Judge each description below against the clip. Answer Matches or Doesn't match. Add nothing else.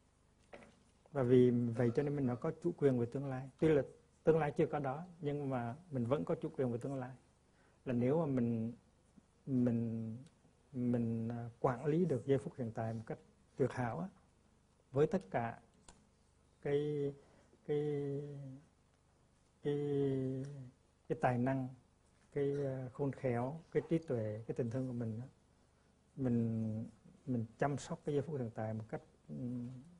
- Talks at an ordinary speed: Doesn't match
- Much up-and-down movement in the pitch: Doesn't match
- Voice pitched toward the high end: Doesn't match